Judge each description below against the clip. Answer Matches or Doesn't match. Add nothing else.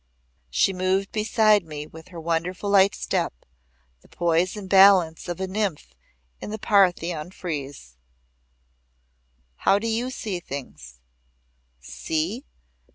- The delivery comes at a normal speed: Doesn't match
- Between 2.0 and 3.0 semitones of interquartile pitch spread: Doesn't match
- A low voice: Doesn't match